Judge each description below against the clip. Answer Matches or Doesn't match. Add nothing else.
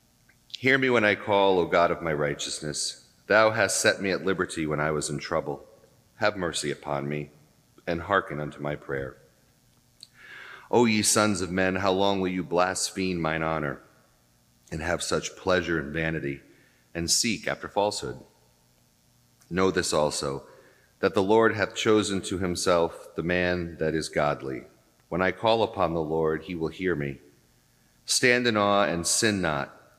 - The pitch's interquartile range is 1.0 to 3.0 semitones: Doesn't match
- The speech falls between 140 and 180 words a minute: Matches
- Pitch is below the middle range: Matches